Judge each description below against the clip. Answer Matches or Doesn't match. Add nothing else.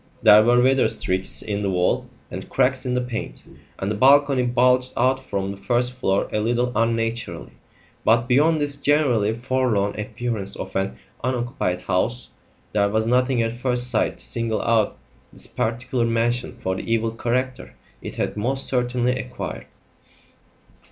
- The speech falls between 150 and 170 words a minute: Matches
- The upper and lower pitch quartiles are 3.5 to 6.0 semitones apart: Doesn't match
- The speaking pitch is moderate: Doesn't match